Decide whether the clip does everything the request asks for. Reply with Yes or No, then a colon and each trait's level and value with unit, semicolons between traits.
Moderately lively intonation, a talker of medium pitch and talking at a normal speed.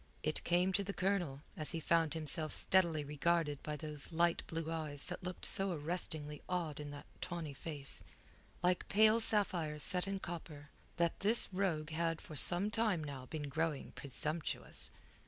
Yes: average, 3.2 semitones; medium, 165 Hz; average, 165 wpm